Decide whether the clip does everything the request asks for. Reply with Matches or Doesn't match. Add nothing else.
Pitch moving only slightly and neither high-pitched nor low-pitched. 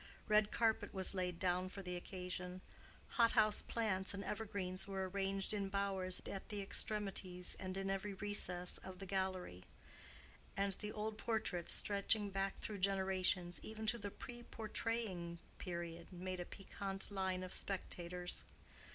Doesn't match